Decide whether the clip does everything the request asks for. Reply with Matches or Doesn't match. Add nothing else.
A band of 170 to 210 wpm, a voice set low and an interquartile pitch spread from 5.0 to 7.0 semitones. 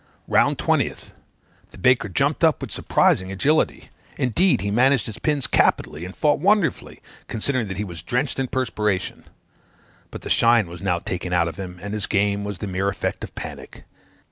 Matches